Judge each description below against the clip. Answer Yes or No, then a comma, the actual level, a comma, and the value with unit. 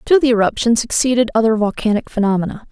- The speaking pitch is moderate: No, high, 230 Hz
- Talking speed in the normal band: Yes, average, 155 wpm